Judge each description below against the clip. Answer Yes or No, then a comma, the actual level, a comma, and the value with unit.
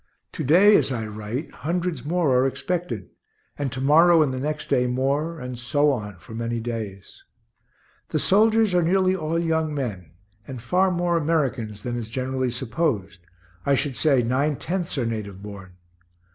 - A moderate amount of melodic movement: No, wide, 6.0 semitones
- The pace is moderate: Yes, average, 170 wpm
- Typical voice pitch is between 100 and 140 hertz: Yes, low, 135 Hz